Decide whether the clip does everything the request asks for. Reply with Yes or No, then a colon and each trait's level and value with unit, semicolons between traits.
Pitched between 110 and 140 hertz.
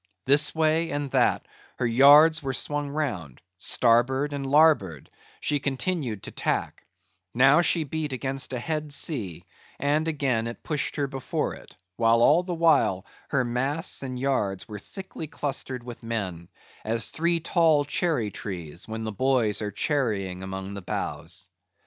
Yes: low, 135 Hz